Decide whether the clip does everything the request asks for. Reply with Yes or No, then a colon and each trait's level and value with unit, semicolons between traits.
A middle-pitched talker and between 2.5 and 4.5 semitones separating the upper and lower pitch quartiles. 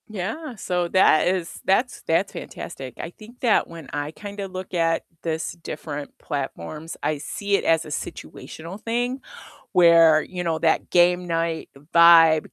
Yes: medium, 170 Hz; average, 3.1 semitones